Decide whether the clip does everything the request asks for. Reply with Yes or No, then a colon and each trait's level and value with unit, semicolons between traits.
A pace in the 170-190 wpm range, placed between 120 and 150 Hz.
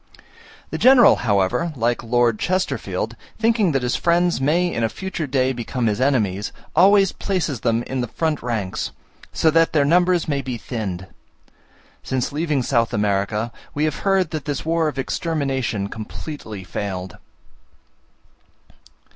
No: average, 145 wpm; low, 135 Hz